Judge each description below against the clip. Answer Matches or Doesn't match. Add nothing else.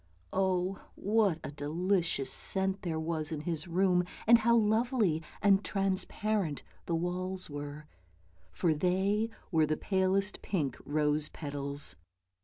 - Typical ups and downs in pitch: Matches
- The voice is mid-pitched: Matches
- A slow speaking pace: Matches